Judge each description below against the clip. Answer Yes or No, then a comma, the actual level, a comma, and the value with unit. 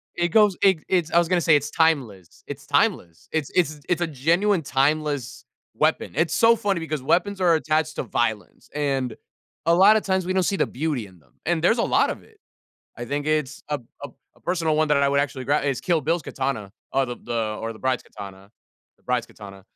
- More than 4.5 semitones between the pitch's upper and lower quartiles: Yes, average, 5.2 semitones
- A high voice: No, medium, 150 Hz